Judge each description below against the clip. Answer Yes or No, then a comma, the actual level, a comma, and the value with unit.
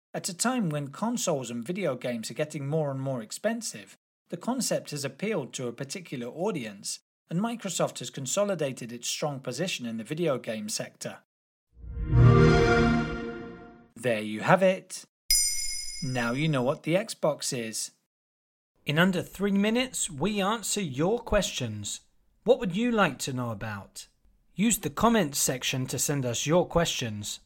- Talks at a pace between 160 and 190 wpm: No, average, 150 wpm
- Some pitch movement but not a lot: No, wide, 8.4 semitones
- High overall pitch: No, medium, 150 Hz